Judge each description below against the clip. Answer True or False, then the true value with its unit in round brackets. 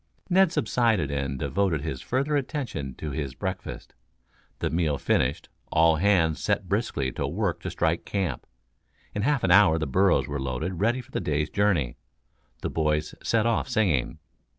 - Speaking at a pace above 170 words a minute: False (165 wpm)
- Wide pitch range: True (5.7 semitones)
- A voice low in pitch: True (85 Hz)